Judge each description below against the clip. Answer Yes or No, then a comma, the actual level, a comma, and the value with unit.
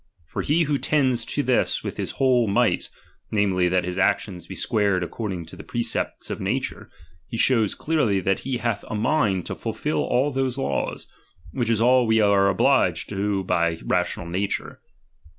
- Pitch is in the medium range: No, low, 105 Hz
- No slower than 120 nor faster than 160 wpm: No, average, 175 wpm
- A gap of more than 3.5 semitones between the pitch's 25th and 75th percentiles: Yes, average, 4.9 semitones